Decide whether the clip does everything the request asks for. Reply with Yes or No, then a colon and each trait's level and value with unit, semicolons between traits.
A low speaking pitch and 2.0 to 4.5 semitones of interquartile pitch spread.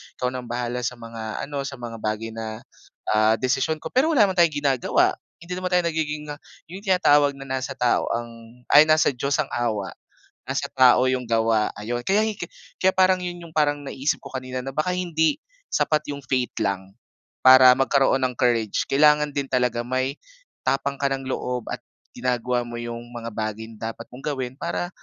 Yes: low, 130 Hz; average, 3.9 semitones